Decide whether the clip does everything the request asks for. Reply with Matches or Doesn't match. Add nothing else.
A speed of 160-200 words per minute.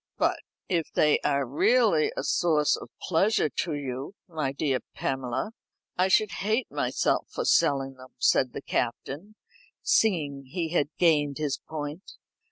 Doesn't match